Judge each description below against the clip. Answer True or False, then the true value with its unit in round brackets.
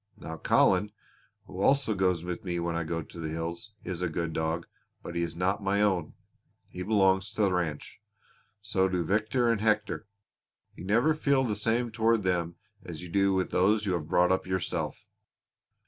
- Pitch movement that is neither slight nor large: True (3.6 semitones)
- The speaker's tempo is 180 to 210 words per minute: True (190 wpm)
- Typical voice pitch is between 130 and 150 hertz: False (95 Hz)